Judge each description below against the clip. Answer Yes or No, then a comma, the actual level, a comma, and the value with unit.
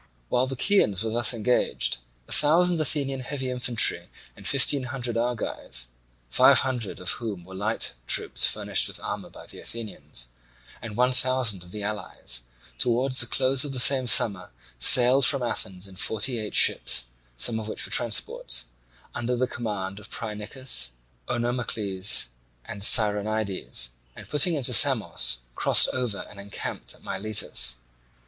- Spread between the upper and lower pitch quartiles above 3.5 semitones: Yes, average, 4.4 semitones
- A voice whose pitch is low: Yes, low, 115 Hz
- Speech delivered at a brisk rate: No, average, 150 wpm